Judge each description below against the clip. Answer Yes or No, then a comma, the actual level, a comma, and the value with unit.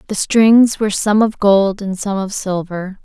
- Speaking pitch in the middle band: No, high, 200 Hz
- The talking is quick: No, average, 195 wpm